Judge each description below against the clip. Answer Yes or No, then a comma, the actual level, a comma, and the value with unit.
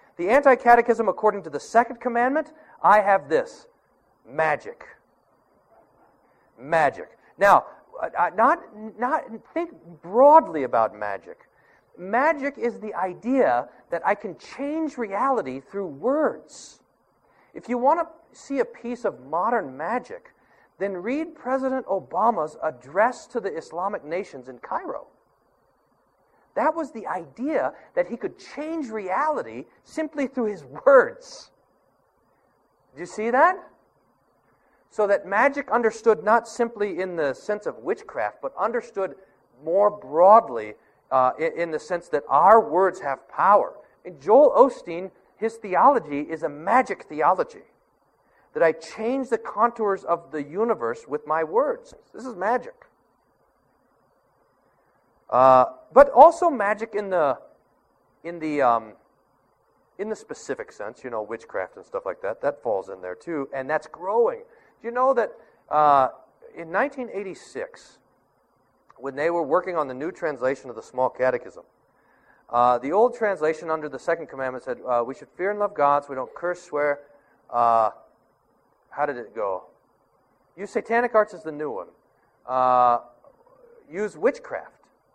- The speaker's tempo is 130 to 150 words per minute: Yes, average, 140 wpm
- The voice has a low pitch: No, high, 215 Hz